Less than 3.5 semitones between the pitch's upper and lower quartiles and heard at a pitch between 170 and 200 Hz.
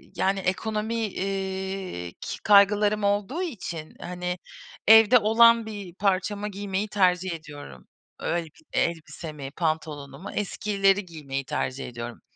No: average, 4.5 semitones; high, 190 Hz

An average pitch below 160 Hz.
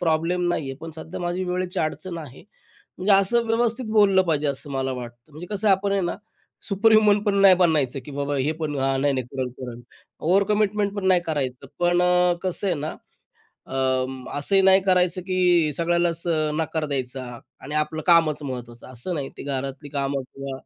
No: medium, 165 Hz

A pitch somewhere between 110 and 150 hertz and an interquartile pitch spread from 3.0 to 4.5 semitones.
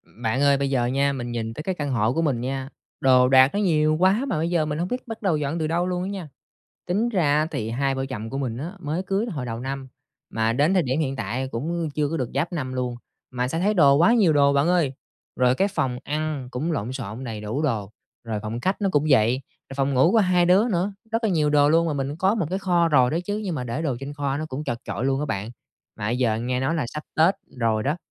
No: medium, 140 Hz; average, 5.1 semitones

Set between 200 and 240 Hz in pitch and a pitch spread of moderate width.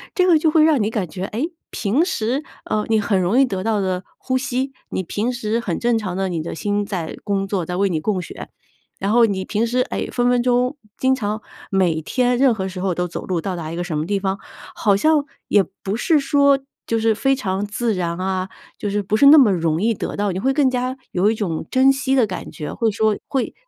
Yes: high, 210 Hz; average, 5.0 semitones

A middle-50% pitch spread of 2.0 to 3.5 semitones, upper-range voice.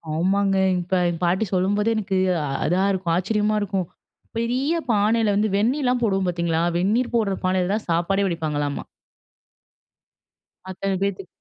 Yes: average, 3.1 semitones; high, 195 Hz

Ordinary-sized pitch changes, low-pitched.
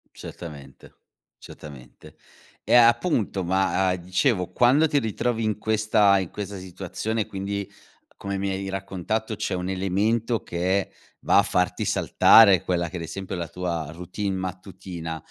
Yes: average, 3.1 semitones; very low, 95 Hz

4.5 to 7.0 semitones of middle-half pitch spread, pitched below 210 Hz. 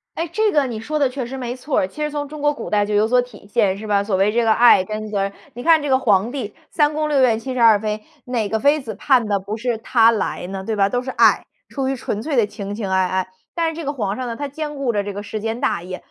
No: average, 5.0 semitones; high, 230 Hz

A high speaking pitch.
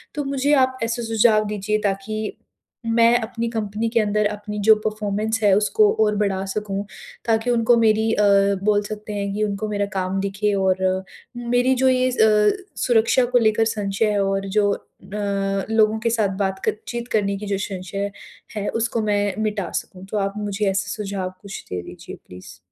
Yes: high, 210 Hz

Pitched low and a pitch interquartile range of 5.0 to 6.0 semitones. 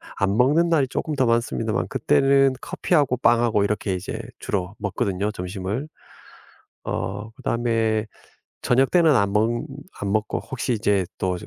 No: low, 110 Hz; average, 4.6 semitones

